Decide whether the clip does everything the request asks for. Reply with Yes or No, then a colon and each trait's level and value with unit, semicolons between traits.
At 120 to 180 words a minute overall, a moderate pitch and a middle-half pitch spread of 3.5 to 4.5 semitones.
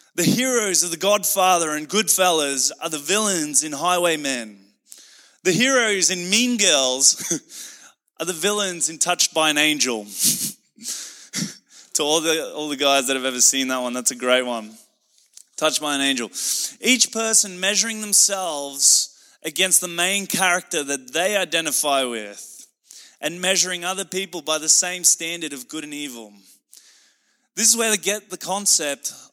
No: average, 155 wpm; medium, 170 Hz; wide, 5.6 semitones